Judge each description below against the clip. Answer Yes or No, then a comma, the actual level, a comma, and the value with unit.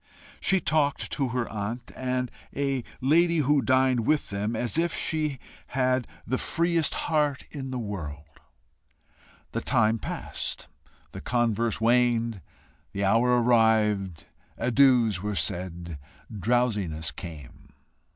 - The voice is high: No, low, 120 Hz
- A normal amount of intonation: Yes, average, 4.4 semitones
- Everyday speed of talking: No, slow, 120 wpm